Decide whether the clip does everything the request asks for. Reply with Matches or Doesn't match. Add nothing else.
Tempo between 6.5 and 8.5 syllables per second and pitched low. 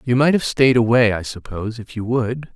Doesn't match